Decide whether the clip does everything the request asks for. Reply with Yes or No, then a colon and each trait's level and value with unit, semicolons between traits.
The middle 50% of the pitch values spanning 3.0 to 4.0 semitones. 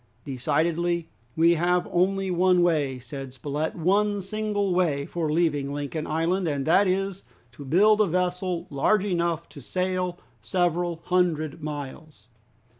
Yes: average, 3.4 semitones